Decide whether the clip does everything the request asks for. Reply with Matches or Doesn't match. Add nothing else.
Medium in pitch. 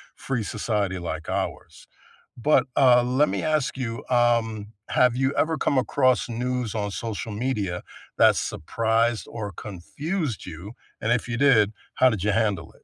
Doesn't match